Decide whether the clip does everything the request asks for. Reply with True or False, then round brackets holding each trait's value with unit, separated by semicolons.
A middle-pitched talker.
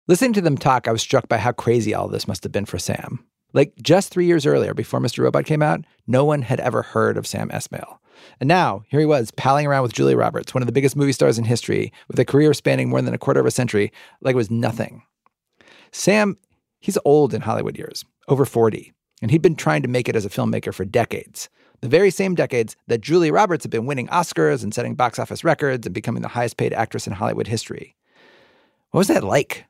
False (130 Hz)